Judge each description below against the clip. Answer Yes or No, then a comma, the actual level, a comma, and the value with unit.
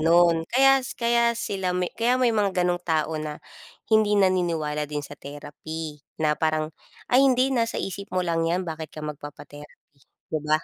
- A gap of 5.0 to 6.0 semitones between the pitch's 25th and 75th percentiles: Yes, average, 5.3 semitones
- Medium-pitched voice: Yes, medium, 170 Hz